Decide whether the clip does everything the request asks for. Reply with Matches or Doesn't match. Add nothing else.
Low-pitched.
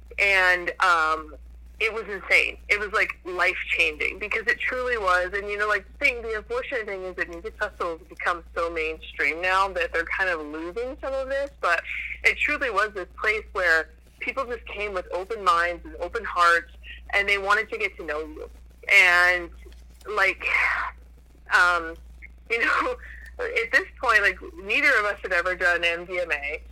Doesn't match